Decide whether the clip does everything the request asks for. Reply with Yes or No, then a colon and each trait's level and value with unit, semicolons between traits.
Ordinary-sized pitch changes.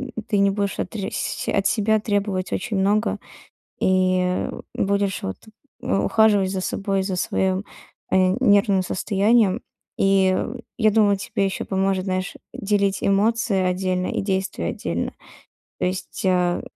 No: narrow, 1.6 semitones